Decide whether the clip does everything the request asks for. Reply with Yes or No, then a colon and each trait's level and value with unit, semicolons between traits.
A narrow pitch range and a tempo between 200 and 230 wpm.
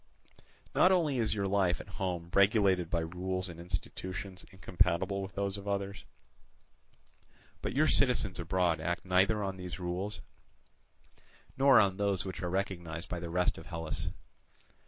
No: narrow, 2.2 semitones; average, 150 wpm